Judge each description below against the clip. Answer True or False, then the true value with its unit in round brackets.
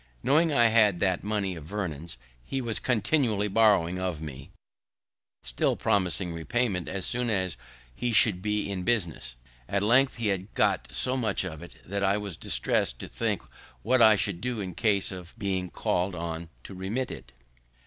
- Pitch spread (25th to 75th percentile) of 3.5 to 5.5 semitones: True (4.2 semitones)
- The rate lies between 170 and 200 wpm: True (175 wpm)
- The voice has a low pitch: True (100 Hz)